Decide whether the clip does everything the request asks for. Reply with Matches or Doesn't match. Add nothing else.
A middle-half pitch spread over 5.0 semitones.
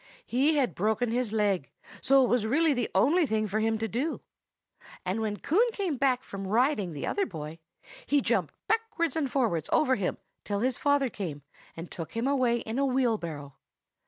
Matches